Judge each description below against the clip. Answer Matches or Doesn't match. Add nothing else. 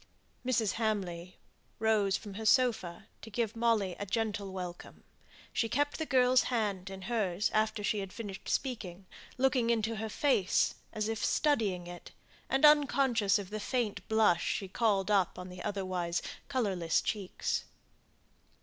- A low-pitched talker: Doesn't match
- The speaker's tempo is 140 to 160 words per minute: Matches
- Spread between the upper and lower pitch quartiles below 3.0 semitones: Doesn't match